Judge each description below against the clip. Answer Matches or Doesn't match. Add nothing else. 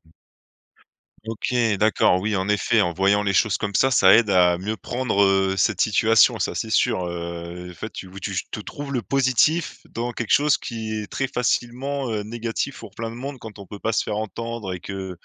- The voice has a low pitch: Matches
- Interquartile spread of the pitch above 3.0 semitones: Matches